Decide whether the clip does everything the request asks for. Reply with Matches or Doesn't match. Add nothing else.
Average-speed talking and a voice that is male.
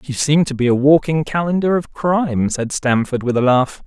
Doesn't match